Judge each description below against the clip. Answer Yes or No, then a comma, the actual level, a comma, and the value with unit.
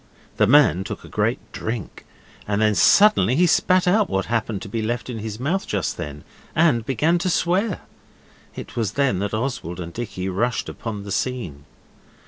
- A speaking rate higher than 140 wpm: Yes, average, 180 wpm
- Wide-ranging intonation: Yes, wide, 6.7 semitones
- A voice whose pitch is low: Yes, low, 115 Hz